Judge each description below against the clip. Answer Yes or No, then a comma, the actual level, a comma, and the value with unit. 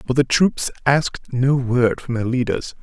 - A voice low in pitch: Yes, low, 125 Hz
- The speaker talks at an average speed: Yes, average, 190 wpm